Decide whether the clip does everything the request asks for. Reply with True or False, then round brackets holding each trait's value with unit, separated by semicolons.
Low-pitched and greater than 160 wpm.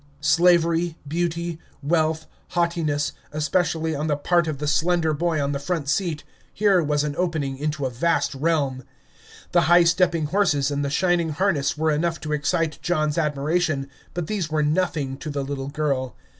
False (155 Hz; 170 wpm)